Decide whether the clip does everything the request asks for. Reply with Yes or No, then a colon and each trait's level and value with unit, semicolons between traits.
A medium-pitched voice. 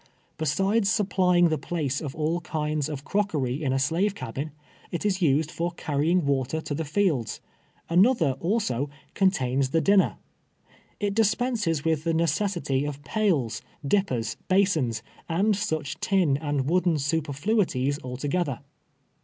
Yes: medium, 160 Hz